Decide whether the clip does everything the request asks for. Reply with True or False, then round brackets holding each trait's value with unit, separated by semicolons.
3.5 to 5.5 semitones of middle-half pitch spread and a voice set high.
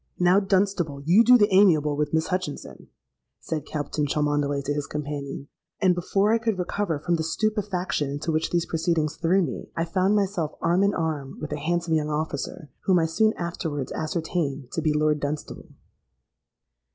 False (3.8 semitones; 165 Hz)